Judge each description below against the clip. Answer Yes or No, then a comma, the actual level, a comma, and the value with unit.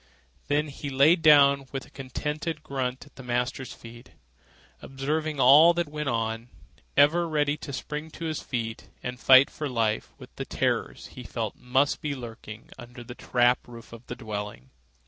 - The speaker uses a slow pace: No, average, 165 wpm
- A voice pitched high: No, low, 135 Hz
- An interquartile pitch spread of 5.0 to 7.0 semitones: No, average, 3.4 semitones